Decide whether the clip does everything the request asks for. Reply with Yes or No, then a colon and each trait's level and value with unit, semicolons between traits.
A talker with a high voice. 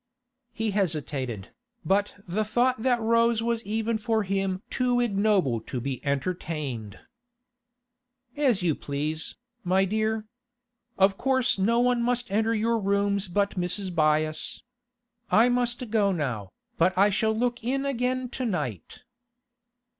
Yes: high, 205 Hz